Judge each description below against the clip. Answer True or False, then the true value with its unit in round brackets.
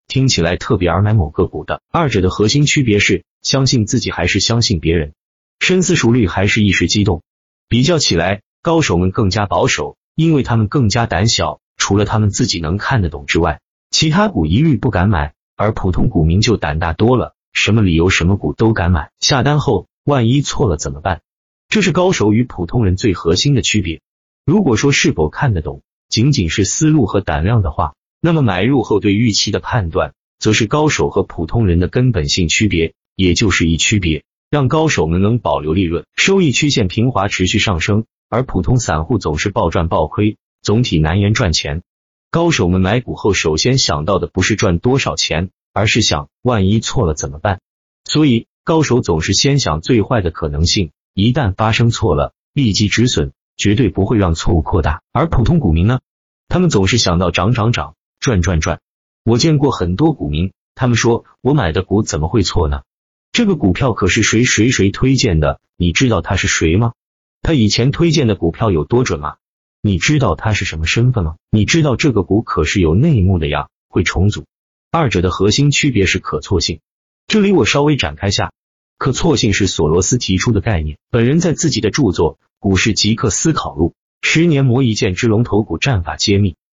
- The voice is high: False (105 Hz)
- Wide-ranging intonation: True (6.1 semitones)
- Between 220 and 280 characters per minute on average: False (290 characters per minute)